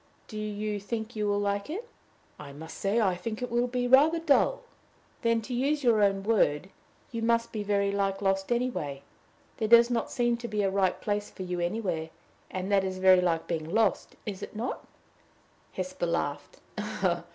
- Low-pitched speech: No, high, 205 Hz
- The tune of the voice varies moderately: Yes, average, 3.8 semitones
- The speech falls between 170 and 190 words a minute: Yes, average, 185 wpm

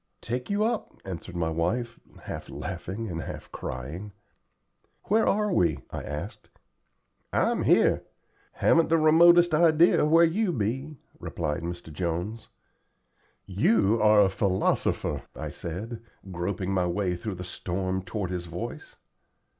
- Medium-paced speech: No, slow, 130 wpm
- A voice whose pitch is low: Yes, low, 100 Hz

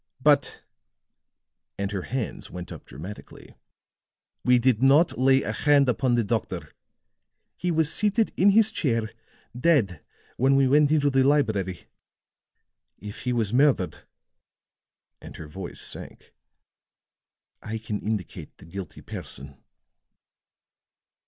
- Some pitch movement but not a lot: No, wide, 6.0 semitones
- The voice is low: Yes, low, 125 Hz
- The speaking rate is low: Yes, slow, 120 wpm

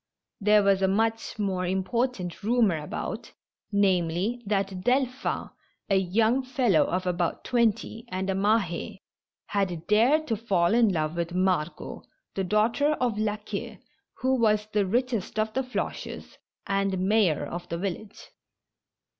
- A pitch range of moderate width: Yes, average, 3.7 semitones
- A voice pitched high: Yes, high, 205 Hz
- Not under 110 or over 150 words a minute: Yes, average, 145 wpm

